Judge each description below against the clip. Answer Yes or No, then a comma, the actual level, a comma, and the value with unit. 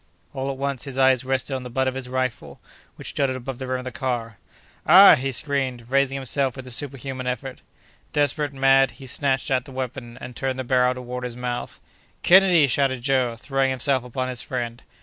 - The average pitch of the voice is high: No, low, 130 Hz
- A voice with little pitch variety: Yes, narrow, 1.4 semitones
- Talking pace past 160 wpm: Yes, fast, 205 wpm